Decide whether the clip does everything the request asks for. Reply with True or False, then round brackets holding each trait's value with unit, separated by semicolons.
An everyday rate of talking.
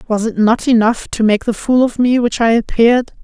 False (240 wpm)